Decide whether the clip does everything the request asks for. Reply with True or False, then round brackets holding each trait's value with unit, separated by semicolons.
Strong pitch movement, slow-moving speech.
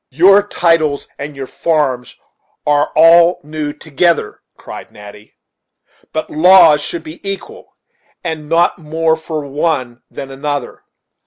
False (2.7 semitones; 125 wpm)